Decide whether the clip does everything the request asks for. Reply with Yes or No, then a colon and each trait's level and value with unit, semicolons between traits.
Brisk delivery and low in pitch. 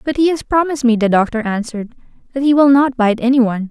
No: fast, 245 wpm; very high, 250 Hz